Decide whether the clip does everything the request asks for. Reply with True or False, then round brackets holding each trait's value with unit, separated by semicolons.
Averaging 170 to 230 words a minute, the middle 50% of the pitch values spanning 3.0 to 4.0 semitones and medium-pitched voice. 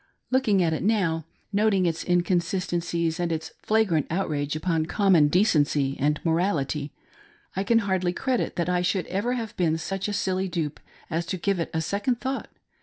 True (175 wpm; 3.7 semitones; 180 Hz)